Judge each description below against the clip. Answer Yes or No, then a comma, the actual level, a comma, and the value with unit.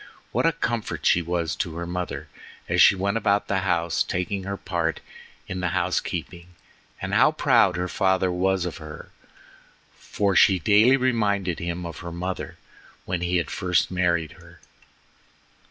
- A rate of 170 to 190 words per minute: No, average, 160 wpm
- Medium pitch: No, very low, 90 Hz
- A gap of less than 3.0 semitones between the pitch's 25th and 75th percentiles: Yes, narrow, 2.4 semitones